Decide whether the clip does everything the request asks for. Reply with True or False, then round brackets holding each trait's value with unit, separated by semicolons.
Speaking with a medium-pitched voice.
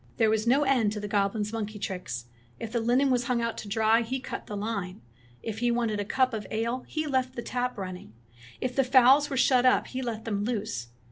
False (230 Hz)